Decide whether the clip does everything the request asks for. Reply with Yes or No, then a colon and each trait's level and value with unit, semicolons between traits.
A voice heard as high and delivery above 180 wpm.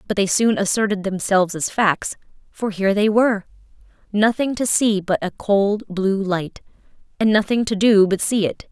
No: high, 205 Hz; average, 170 wpm